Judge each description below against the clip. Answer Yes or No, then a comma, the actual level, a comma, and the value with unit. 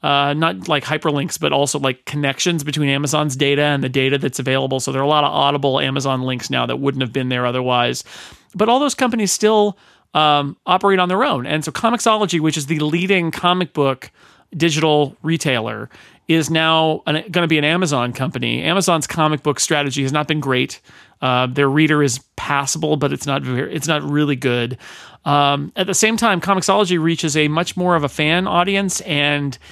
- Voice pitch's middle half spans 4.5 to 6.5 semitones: No, average, 3.7 semitones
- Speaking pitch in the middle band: Yes, medium, 150 Hz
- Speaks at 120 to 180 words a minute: No, average, 195 wpm